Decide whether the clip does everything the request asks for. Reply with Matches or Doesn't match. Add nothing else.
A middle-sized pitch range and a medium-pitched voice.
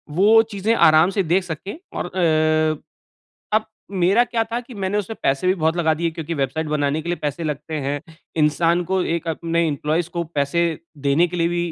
Matches